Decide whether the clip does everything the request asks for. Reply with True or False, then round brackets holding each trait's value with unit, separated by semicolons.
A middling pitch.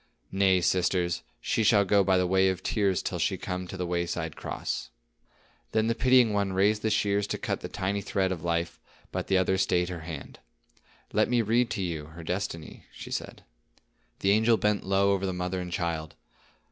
False (95 Hz)